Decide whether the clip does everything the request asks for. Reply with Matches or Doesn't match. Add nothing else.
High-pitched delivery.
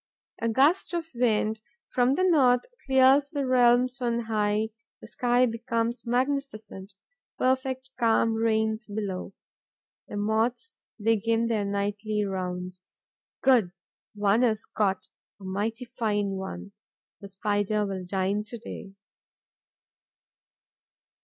Matches